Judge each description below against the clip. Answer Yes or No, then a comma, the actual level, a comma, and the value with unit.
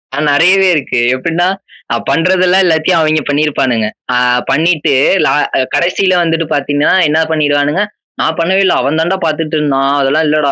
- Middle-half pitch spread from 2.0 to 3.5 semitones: Yes, average, 3.1 semitones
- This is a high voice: No, medium, 155 Hz